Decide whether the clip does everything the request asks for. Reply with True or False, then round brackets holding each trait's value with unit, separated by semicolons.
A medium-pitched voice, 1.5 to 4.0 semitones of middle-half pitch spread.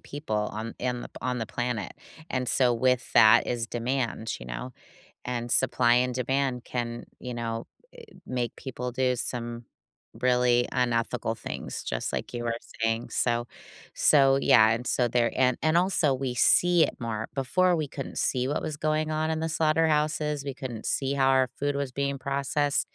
False (125 Hz; 2.9 semitones)